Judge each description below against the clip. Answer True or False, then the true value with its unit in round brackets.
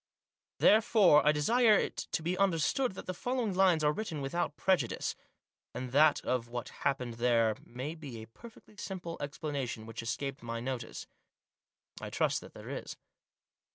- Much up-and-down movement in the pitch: True (7.2 semitones)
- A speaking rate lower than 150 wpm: False (155 wpm)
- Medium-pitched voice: True (150 Hz)